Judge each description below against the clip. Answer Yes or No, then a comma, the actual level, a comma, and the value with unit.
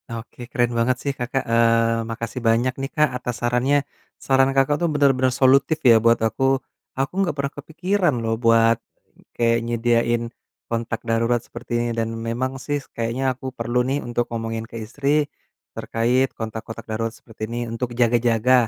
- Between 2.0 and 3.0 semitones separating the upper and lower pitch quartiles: Yes, narrow, 2.5 semitones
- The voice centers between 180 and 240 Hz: No, low, 120 Hz